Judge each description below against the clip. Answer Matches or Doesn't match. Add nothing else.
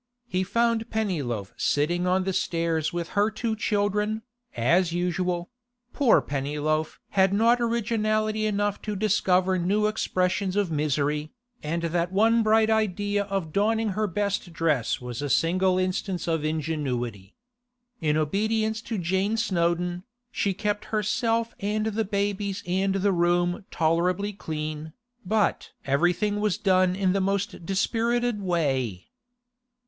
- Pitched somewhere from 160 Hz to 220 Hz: Matches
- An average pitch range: Matches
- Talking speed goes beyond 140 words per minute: Doesn't match